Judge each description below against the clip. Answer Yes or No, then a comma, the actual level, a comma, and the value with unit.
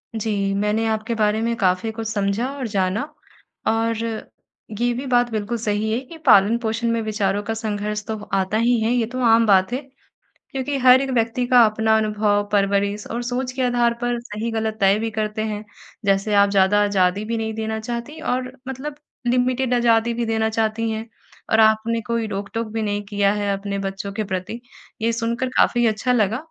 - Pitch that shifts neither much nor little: No, narrow, 2.3 semitones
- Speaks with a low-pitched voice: No, high, 220 Hz